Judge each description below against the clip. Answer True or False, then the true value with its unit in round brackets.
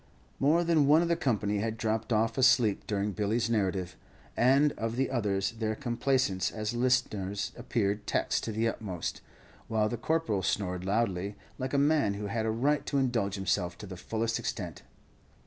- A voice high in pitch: False (110 Hz)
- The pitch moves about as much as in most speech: True (4.0 semitones)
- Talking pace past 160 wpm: True (175 wpm)